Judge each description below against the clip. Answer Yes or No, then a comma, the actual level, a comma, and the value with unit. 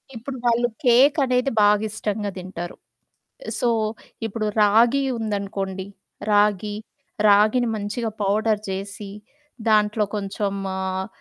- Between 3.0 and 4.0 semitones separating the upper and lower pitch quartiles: No, narrow, 2.5 semitones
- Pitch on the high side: Yes, high, 210 Hz